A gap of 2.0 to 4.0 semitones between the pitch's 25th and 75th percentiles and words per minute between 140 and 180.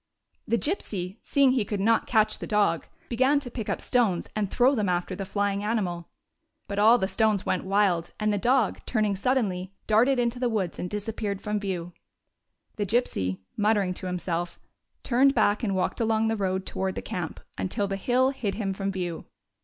No: average, 3.4 semitones; average, 190 wpm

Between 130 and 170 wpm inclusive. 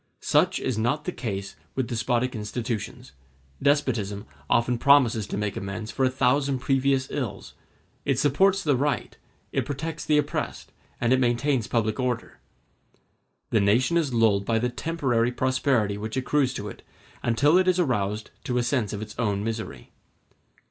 Yes: average, 160 wpm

